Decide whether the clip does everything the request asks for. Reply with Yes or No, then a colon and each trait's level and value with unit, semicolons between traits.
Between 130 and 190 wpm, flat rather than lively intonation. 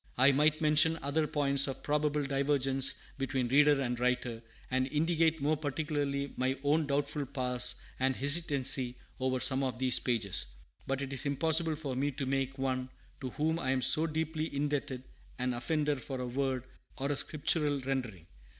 Yes: average, 170 wpm; narrow, 2.3 semitones